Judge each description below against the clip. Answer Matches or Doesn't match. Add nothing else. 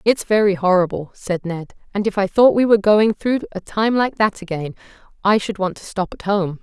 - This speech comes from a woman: Matches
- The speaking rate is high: Matches